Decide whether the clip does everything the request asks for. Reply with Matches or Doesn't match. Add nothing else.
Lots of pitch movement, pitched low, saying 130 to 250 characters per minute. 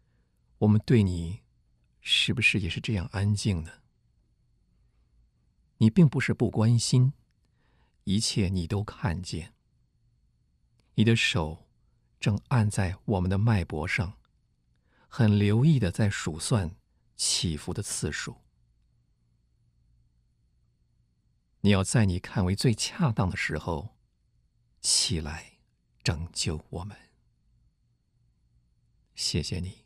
Matches